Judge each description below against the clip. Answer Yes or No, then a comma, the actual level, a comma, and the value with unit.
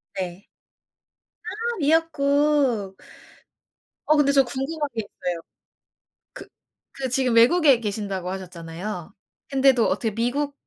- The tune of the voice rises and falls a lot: Yes, wide, 6.3 semitones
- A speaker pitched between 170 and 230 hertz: No, very high, 250 Hz